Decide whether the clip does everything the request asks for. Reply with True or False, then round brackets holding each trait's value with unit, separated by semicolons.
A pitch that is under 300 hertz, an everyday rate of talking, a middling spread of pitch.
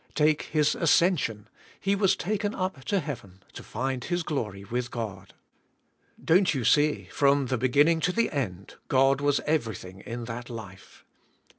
False (135 Hz; 155 wpm; 6.0 semitones)